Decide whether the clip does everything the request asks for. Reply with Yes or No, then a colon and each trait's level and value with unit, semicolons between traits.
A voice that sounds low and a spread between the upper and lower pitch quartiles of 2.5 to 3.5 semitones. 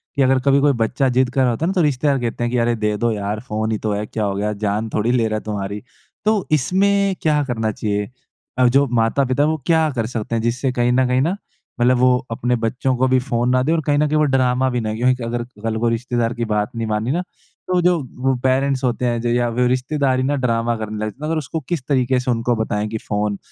Yes: low, 125 Hz; average, 3.2 semitones